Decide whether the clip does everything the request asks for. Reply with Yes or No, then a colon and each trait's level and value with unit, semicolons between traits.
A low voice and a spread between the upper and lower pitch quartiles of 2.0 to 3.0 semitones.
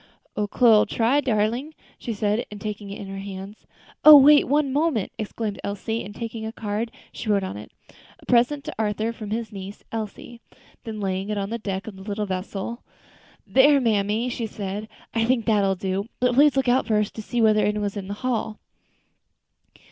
No: high, 215 Hz; average, 2.7 semitones